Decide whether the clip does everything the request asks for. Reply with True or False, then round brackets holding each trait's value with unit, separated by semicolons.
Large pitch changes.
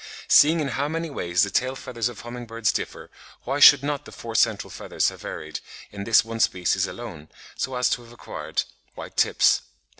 False (3.6 semitones)